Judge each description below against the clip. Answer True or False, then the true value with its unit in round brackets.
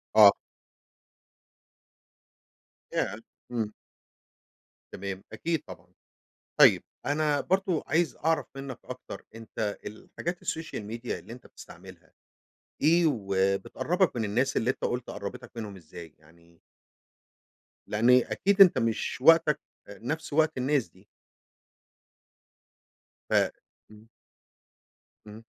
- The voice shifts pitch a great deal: True (7.1 semitones)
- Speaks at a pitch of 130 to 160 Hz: False (120 Hz)